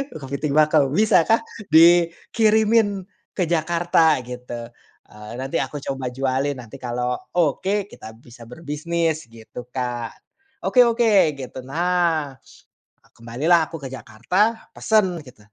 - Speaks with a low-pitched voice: No, medium, 150 Hz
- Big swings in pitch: Yes, wide, 5.9 semitones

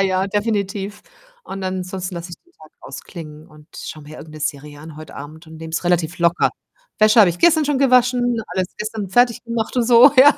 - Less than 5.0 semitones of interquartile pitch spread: No, wide, 6.4 semitones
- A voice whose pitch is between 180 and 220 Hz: Yes, high, 190 Hz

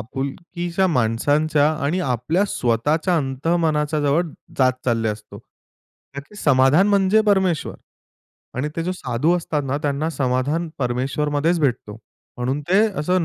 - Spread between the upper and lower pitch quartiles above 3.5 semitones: Yes, average, 4.8 semitones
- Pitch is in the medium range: Yes, medium, 150 Hz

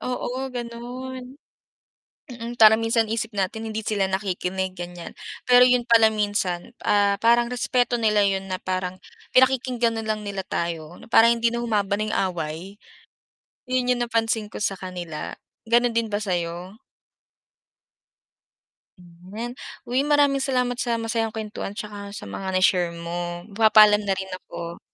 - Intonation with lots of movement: No, average, 4.1 semitones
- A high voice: Yes, high, 215 Hz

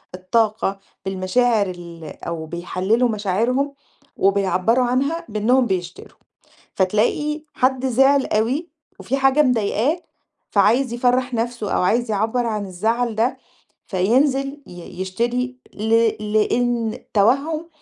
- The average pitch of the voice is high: Yes, high, 230 Hz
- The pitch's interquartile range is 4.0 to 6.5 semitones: Yes, average, 4.5 semitones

